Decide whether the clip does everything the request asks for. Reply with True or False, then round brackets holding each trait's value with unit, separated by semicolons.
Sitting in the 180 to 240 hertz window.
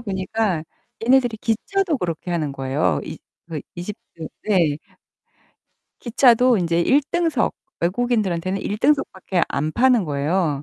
True (190 Hz)